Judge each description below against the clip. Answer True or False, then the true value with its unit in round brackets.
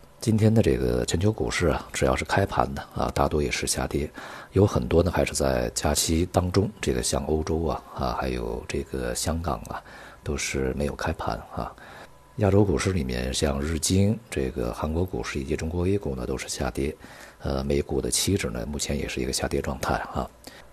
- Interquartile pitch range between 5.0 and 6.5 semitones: True (5.3 semitones)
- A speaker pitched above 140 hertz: False (75 Hz)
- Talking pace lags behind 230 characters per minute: False (285 characters per minute)